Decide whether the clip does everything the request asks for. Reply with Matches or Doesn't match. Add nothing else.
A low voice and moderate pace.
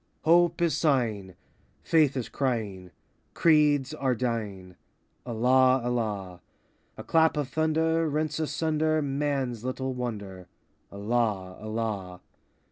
Doesn't match